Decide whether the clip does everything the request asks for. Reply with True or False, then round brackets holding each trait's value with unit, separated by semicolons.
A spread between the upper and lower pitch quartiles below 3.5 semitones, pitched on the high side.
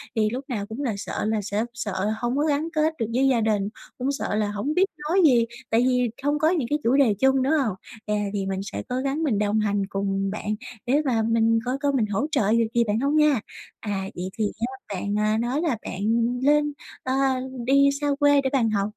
False (4.9 semitones; 235 Hz)